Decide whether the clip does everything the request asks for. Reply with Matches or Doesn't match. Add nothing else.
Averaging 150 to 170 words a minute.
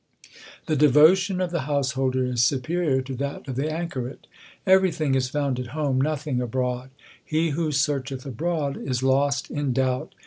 Matches